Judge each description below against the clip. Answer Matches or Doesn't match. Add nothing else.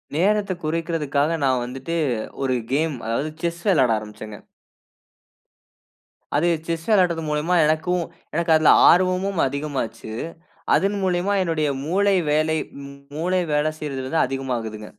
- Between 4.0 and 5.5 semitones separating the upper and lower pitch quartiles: Matches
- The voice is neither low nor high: Matches